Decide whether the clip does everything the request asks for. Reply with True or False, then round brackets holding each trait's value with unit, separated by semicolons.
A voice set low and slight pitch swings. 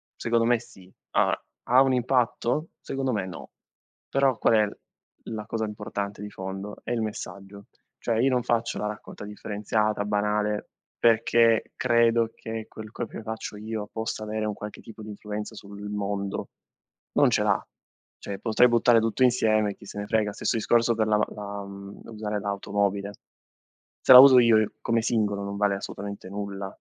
True (105 Hz; 2.1 semitones)